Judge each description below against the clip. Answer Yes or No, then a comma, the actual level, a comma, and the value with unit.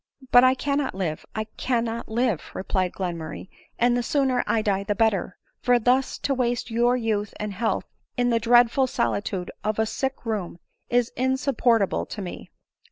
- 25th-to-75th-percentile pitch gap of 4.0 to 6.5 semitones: No, average, 3.4 semitones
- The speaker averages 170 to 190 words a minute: Yes, average, 180 wpm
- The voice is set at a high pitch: Yes, high, 230 Hz